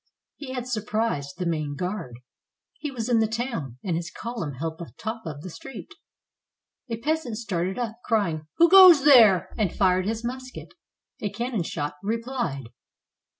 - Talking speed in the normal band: Yes, average, 165 wpm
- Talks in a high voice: Yes, high, 215 Hz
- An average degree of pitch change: No, wide, 6.3 semitones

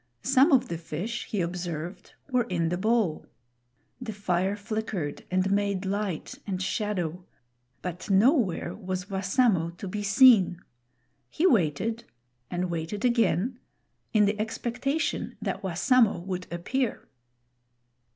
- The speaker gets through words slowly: Yes, slow, 120 wpm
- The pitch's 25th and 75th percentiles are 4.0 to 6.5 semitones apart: Yes, average, 4.5 semitones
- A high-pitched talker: Yes, high, 200 Hz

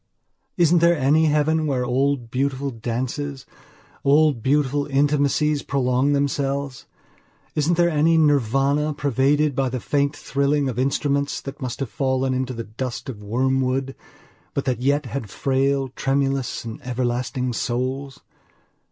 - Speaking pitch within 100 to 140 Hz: Yes, low, 135 Hz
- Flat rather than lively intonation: Yes, narrow, 2.1 semitones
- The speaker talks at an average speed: No, slow, 130 wpm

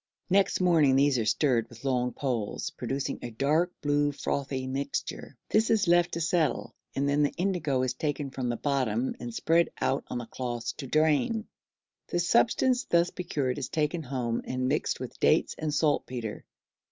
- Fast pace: No, average, 170 wpm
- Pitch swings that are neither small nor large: Yes, average, 4.6 semitones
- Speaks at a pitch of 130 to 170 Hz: Yes, medium, 140 Hz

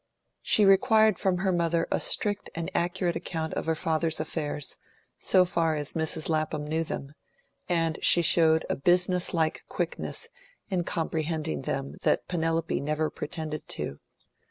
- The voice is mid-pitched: Yes, medium, 165 Hz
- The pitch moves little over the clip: Yes, narrow, 2.1 semitones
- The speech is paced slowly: No, average, 155 wpm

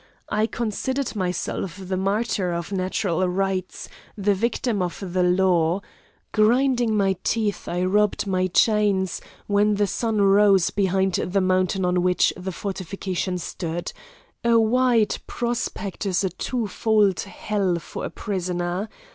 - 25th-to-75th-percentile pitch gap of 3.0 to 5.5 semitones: No, narrow, 2.6 semitones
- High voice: Yes, high, 195 Hz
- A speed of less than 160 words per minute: Yes, slow, 135 wpm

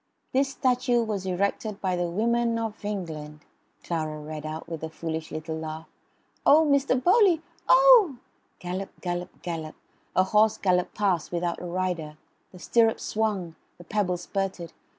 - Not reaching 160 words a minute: Yes, average, 150 wpm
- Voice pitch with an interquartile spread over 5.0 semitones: Yes, wide, 5.4 semitones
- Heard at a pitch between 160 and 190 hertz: Yes, medium, 185 Hz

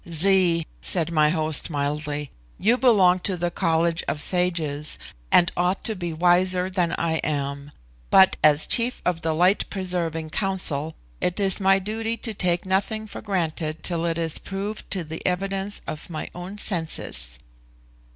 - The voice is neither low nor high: Yes, medium, 175 Hz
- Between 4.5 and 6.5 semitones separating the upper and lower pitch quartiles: No, average, 3.2 semitones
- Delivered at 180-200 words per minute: No, average, 160 wpm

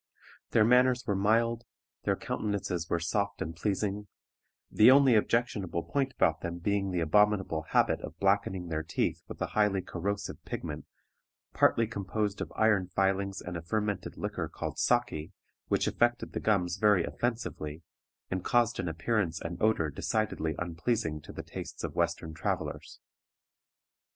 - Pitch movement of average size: Yes, average, 4.1 semitones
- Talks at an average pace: Yes, average, 150 wpm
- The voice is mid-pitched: No, low, 100 Hz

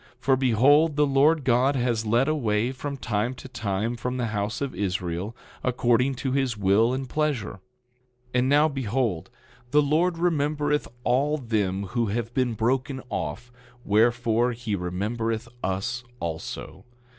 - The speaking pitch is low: Yes, low, 120 Hz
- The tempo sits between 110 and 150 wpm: Yes, average, 145 wpm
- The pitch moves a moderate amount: Yes, average, 4.0 semitones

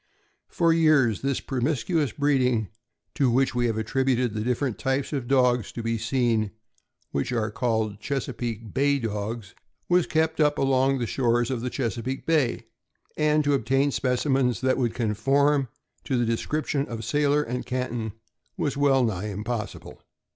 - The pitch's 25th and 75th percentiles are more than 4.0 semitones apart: No, average, 3.4 semitones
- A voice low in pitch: Yes, low, 125 Hz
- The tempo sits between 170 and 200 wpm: No, average, 160 wpm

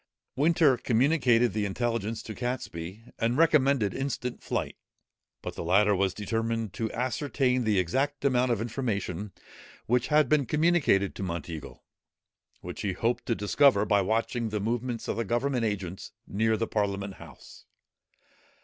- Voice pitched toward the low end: Yes, low, 115 Hz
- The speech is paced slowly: No, average, 145 wpm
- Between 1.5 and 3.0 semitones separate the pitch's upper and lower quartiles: No, average, 4.1 semitones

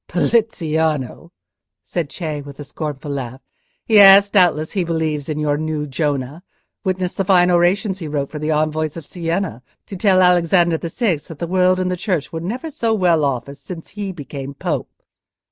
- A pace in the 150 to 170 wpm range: No, average, 180 wpm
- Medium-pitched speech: Yes, medium, 165 Hz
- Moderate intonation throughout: Yes, average, 3.7 semitones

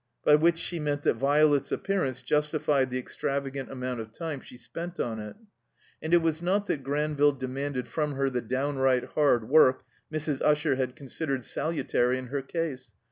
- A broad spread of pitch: No, average, 3.0 semitones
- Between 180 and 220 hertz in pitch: No, medium, 140 Hz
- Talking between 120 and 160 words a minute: No, average, 175 wpm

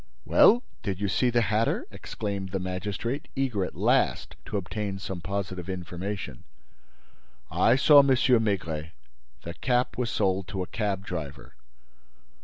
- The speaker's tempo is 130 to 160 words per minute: Yes, average, 140 wpm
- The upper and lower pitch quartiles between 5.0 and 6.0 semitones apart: No, average, 3.9 semitones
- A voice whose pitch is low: Yes, low, 100 Hz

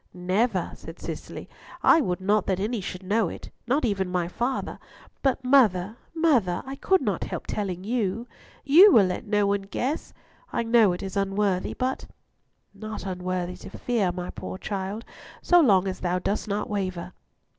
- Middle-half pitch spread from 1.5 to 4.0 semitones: No, average, 4.4 semitones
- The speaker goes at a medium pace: Yes, average, 170 wpm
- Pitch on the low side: No, high, 200 Hz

